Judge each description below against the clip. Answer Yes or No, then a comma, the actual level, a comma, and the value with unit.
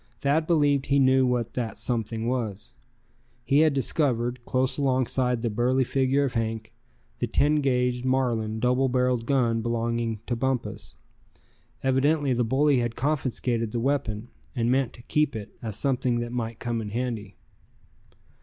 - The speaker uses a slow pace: No, average, 155 wpm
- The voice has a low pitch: Yes, low, 125 Hz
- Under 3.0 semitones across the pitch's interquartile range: Yes, narrow, 2.5 semitones